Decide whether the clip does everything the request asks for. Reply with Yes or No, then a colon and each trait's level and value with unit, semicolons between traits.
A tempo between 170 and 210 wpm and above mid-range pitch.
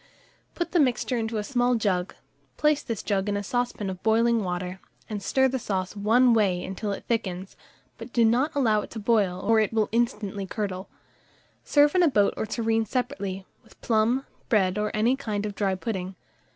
Yes: average, 190 wpm; high, 215 Hz